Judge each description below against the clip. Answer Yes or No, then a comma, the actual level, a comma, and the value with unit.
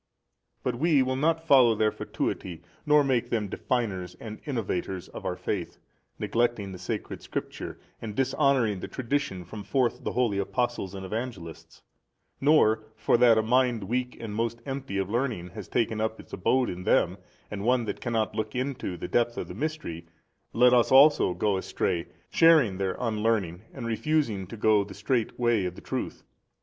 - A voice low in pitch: Yes, low, 115 Hz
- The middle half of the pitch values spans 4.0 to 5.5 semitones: Yes, average, 4.4 semitones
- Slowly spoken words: No, average, 180 wpm